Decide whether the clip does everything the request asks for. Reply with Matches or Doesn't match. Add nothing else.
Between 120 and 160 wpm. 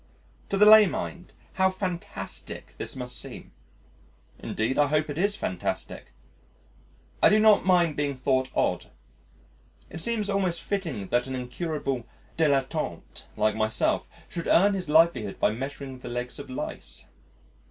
Matches